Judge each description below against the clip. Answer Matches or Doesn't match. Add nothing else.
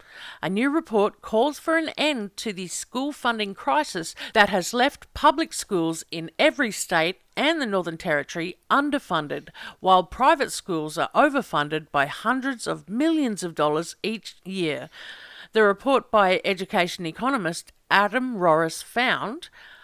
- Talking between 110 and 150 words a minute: Matches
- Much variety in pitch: Matches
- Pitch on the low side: Doesn't match